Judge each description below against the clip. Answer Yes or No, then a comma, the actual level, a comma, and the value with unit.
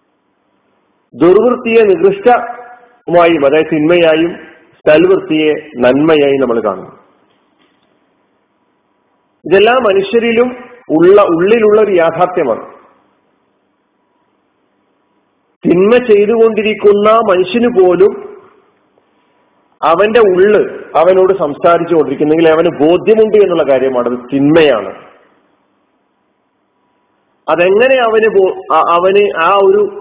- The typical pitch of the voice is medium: No, high, 205 Hz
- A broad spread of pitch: Yes, wide, 6.8 semitones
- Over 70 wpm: No, average, 65 wpm